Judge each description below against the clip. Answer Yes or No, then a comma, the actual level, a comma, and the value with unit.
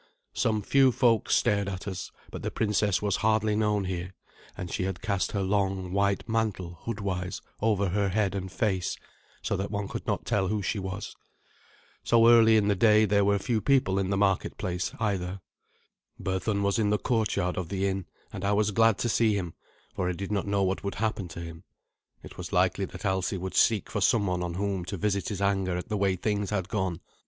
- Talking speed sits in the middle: No, fast, 210 wpm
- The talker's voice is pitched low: Yes, low, 100 Hz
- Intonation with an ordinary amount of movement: No, narrow, 2.1 semitones